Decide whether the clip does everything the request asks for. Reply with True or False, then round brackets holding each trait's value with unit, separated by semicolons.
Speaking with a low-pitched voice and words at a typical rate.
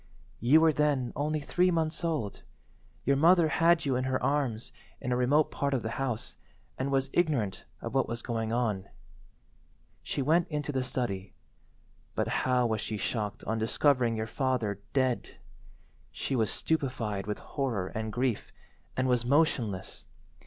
True (130 Hz; 160 wpm)